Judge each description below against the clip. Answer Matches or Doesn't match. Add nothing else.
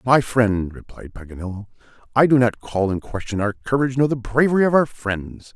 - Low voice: Matches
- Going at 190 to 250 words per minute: Matches